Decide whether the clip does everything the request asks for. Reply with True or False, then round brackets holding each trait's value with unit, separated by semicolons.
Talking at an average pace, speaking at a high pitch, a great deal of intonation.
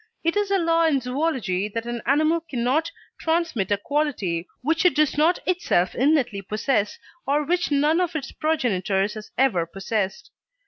True (165 wpm; 280 Hz; 7.5 semitones)